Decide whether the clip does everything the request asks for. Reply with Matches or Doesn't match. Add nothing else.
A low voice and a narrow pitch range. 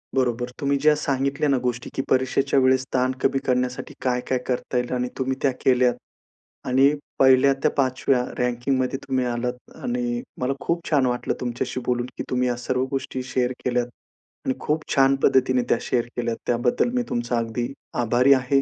Matches